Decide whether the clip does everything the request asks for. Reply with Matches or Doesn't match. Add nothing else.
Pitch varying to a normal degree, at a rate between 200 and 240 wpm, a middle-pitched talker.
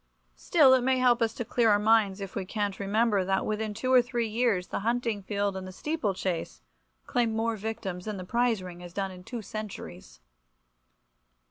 Doesn't match